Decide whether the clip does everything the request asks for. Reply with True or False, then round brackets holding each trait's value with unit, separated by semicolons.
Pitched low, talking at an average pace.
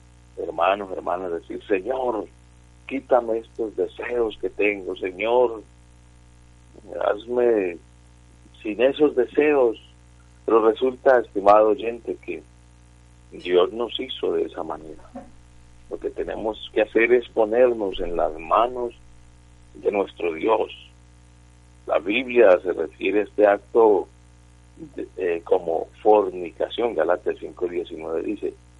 False (100 Hz; 110 wpm)